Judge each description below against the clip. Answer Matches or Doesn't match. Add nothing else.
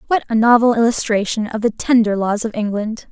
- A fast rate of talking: Doesn't match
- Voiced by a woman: Matches